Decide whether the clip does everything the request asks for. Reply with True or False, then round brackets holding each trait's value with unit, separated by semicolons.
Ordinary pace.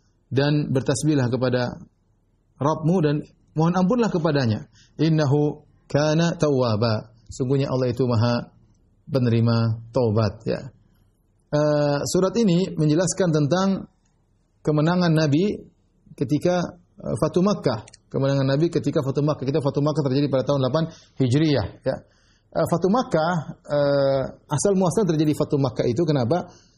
True (120 wpm)